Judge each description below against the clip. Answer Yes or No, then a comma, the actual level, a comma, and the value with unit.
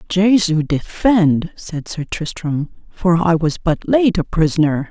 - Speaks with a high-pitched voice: No, medium, 170 Hz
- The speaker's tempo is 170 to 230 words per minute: No, average, 145 wpm